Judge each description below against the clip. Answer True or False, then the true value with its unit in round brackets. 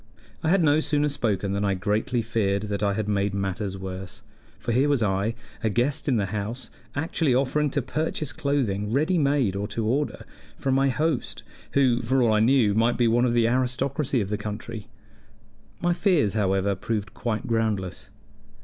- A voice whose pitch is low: True (115 Hz)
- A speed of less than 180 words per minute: False (185 wpm)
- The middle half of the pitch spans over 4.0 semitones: True (5.2 semitones)